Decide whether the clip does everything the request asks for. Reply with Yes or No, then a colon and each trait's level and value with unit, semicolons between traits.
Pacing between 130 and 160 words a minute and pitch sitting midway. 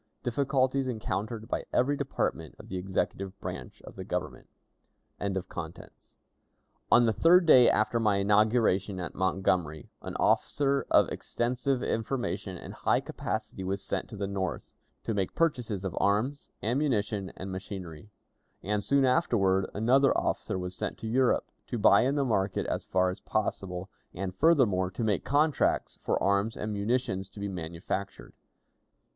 No: average, 150 wpm; low, 105 Hz